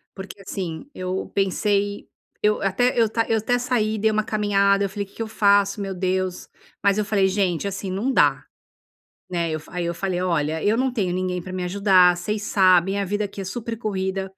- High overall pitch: Yes, high, 195 Hz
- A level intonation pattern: Yes, narrow, 2.3 semitones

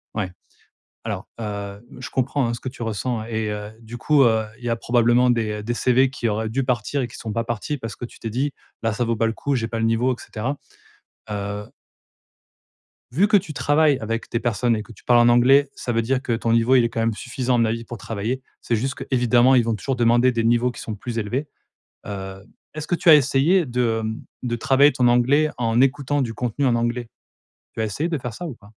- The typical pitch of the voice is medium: No, low, 120 Hz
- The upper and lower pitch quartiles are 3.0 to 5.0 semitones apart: No, narrow, 2.6 semitones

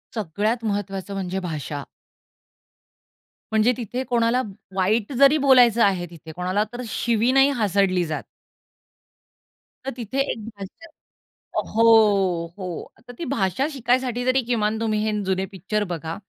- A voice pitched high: Yes, high, 215 Hz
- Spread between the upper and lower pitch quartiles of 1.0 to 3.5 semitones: No, average, 4.4 semitones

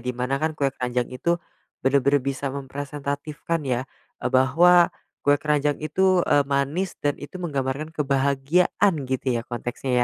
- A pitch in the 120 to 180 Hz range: Yes, medium, 140 Hz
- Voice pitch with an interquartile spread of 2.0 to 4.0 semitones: Yes, average, 2.8 semitones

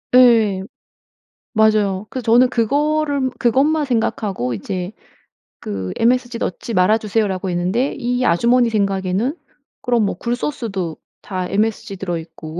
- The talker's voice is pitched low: No, high, 220 Hz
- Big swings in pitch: No, average, 4.8 semitones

